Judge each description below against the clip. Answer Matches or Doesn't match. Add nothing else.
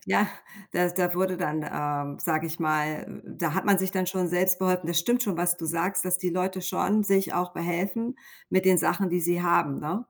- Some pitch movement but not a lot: Doesn't match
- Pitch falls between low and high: Matches